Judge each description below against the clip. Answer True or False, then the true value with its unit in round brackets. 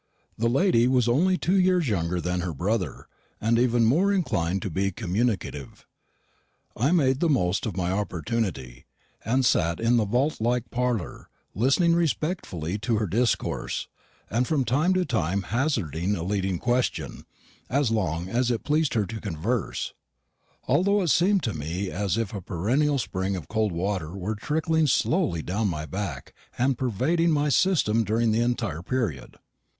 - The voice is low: True (115 Hz)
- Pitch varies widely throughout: True (6.4 semitones)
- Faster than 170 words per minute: False (160 wpm)